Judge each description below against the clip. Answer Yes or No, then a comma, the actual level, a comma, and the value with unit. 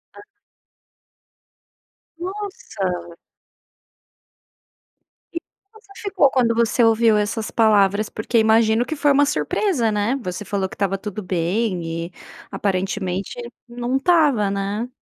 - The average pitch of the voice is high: Yes, high, 220 Hz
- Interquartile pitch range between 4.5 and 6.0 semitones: Yes, wide, 5.4 semitones